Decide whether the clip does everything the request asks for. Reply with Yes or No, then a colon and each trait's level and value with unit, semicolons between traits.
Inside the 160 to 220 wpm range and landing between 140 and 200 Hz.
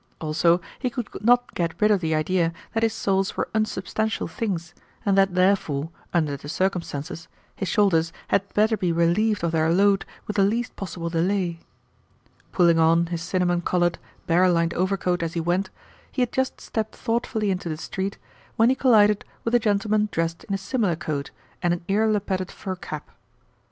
Yes: average, 180 wpm; medium, 185 Hz